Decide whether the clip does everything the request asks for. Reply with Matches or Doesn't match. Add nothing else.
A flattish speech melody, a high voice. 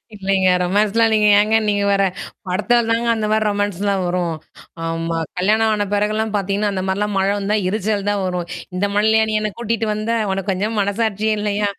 Matches